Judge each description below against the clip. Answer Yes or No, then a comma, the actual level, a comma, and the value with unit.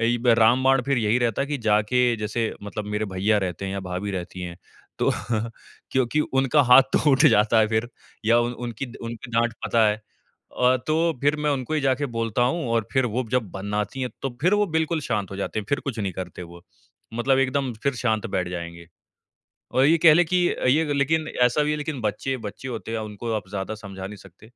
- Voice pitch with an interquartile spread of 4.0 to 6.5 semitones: Yes, average, 4.5 semitones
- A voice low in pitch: Yes, low, 115 Hz